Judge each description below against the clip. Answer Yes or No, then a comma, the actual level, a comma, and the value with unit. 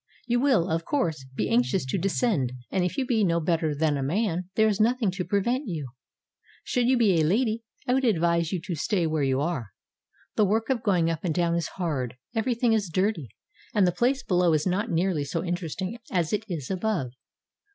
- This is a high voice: No, medium, 180 Hz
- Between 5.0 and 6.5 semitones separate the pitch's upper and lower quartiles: Yes, average, 5.3 semitones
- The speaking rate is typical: No, fast, 215 wpm